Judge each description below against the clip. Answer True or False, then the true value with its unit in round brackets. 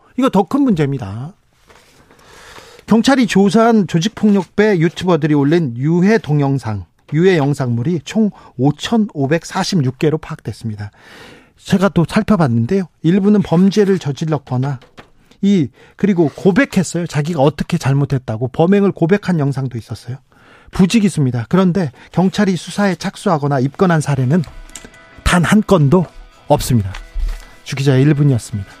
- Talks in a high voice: False (165 Hz)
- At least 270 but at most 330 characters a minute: True (300 characters per minute)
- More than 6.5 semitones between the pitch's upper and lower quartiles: False (6.2 semitones)